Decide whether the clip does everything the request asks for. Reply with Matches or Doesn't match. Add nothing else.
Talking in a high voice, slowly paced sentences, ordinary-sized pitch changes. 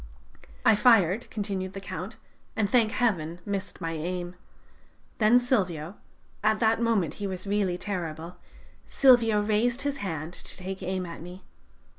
Doesn't match